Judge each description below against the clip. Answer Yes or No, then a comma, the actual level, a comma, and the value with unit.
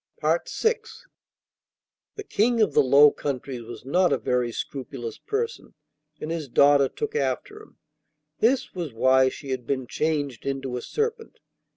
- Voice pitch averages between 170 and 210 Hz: No, medium, 140 Hz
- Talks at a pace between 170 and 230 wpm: No, average, 150 wpm